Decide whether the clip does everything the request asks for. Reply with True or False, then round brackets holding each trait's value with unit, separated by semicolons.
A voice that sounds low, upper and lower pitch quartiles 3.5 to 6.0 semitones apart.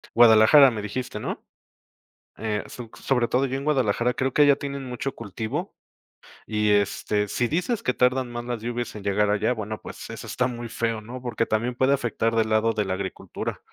False (120 Hz; 2.8 semitones)